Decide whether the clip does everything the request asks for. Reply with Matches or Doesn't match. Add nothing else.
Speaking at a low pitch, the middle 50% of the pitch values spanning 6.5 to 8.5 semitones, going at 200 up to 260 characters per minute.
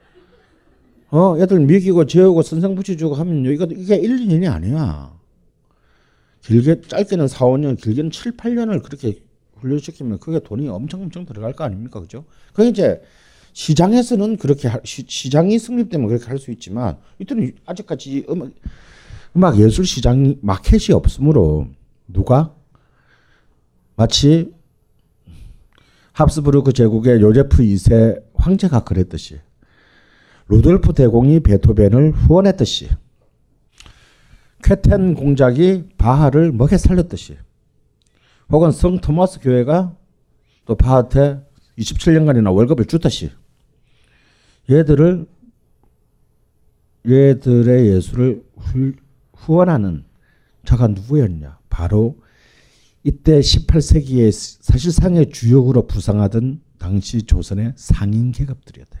Matches